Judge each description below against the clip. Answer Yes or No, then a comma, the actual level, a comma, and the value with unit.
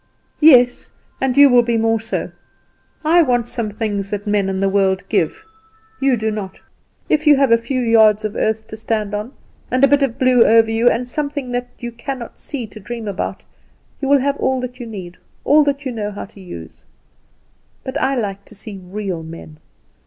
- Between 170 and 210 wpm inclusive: Yes, average, 195 wpm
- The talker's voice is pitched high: Yes, high, 230 Hz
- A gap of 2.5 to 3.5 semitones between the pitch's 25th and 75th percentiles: No, average, 4.0 semitones